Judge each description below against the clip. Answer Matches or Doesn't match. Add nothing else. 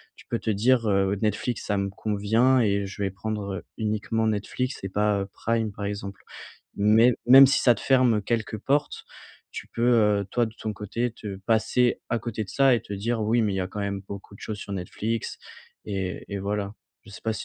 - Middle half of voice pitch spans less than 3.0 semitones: Matches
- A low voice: Matches